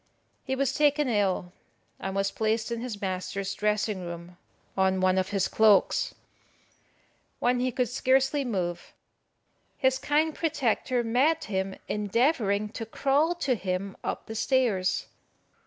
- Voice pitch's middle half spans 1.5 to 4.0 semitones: No, average, 5.3 semitones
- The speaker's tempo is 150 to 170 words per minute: No, slow, 135 wpm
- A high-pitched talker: Yes, high, 220 Hz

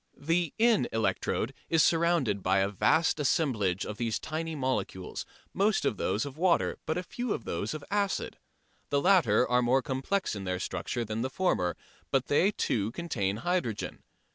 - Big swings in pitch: Yes, wide, 8.0 semitones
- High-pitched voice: No, low, 135 Hz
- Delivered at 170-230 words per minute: Yes, average, 175 wpm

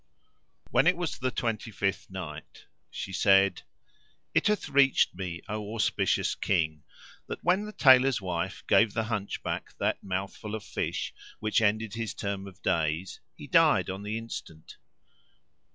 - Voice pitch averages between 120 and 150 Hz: No, low, 100 Hz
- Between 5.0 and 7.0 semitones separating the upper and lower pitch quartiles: No, average, 3.4 semitones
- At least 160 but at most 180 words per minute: No, average, 150 wpm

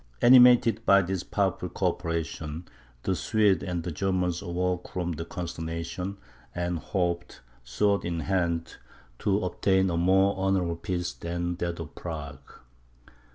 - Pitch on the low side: Yes, very low, 90 Hz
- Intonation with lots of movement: No, narrow, 2.4 semitones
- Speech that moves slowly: Yes, slow, 130 wpm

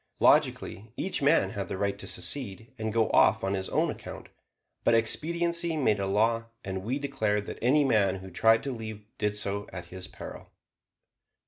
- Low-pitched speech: Yes, low, 110 Hz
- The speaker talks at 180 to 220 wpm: Yes, average, 185 wpm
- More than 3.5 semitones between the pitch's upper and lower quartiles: Yes, average, 4.8 semitones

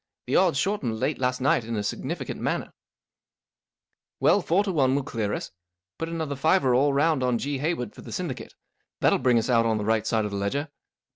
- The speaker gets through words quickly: Yes, fast, 220 wpm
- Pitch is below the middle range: Yes, low, 130 Hz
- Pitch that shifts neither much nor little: Yes, average, 4.9 semitones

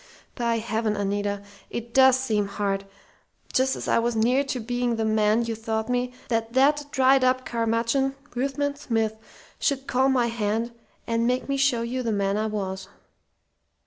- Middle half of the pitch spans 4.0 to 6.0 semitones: No, average, 2.9 semitones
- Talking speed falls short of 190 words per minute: Yes, average, 170 wpm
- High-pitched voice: Yes, high, 235 Hz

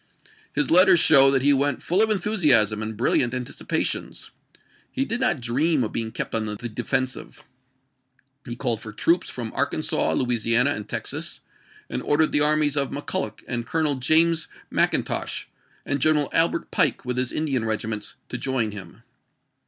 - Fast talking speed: No, average, 165 wpm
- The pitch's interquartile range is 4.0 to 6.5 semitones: Yes, average, 5.0 semitones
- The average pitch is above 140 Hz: No, low, 135 Hz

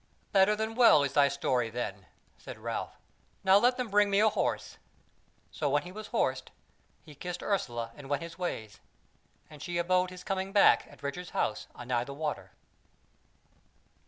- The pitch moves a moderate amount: No, wide, 5.9 semitones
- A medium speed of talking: Yes, average, 170 wpm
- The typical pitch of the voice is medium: Yes, medium, 175 Hz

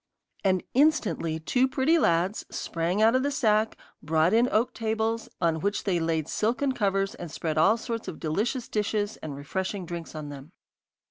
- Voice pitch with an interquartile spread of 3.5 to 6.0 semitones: Yes, wide, 5.6 semitones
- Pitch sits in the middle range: No, high, 200 Hz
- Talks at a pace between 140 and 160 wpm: No, average, 175 wpm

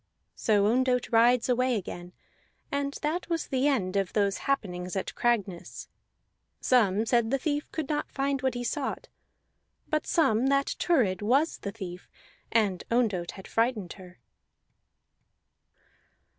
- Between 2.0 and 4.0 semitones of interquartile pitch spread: No, wide, 5.5 semitones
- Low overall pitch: No, high, 235 Hz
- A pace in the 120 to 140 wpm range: Yes, slow, 135 wpm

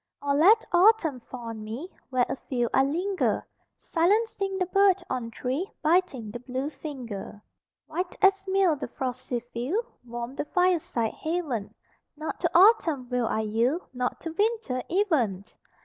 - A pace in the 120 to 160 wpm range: Yes, average, 150 wpm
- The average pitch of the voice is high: Yes, very high, 290 Hz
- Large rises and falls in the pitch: Yes, wide, 7.1 semitones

